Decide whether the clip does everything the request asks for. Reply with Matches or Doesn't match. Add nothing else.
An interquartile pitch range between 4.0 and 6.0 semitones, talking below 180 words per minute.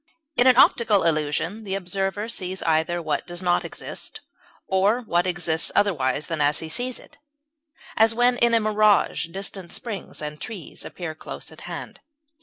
Matches